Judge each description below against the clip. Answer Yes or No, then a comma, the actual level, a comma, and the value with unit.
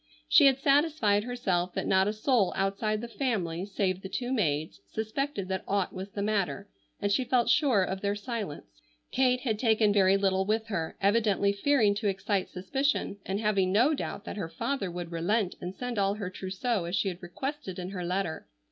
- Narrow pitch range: No, average, 3.7 semitones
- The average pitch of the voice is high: Yes, high, 200 Hz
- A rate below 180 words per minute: No, average, 195 wpm